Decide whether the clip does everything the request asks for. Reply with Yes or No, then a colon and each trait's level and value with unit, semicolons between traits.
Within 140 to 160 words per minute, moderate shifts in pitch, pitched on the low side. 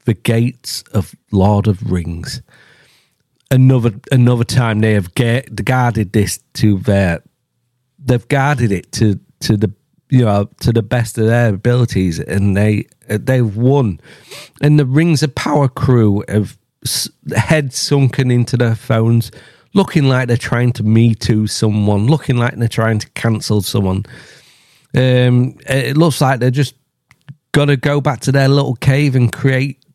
Yes: average, 155 wpm; average, 3.8 semitones; low, 120 Hz